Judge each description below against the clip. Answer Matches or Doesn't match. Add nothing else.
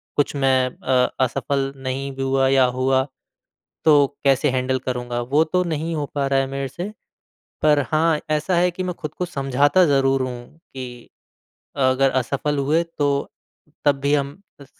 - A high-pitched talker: Doesn't match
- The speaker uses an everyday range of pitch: Doesn't match